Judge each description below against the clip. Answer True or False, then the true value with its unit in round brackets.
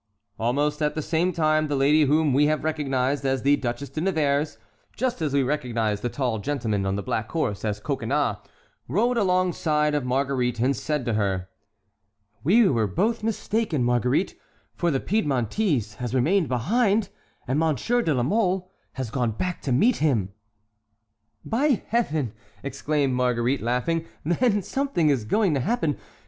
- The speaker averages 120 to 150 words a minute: False (160 wpm)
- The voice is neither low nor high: True (145 Hz)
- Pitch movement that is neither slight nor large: False (5.9 semitones)